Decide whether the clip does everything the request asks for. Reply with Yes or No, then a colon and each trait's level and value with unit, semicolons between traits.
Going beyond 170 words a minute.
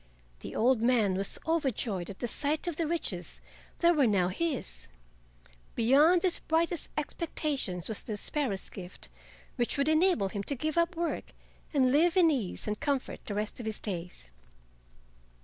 No: average, 165 wpm